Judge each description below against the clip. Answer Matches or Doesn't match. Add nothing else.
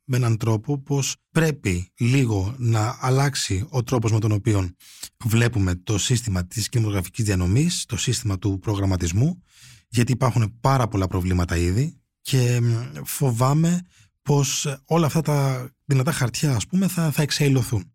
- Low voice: Matches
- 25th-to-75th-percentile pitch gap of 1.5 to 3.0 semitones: Doesn't match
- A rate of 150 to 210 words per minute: Doesn't match